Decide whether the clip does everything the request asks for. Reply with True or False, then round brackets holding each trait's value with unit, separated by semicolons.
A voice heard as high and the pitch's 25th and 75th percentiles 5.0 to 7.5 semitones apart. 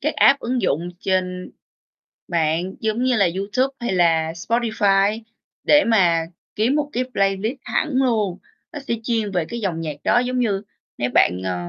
True (200 Hz; 5.4 semitones)